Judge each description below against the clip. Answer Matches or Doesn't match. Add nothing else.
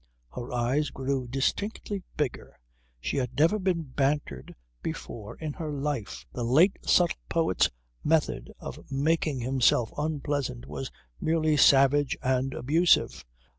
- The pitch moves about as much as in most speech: Matches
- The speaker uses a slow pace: Matches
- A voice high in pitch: Doesn't match